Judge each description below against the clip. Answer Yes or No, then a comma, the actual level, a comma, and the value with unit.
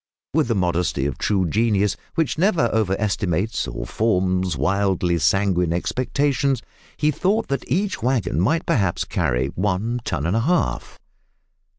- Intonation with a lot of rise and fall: Yes, wide, 6.4 semitones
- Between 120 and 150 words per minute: Yes, average, 145 wpm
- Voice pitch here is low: Yes, low, 100 Hz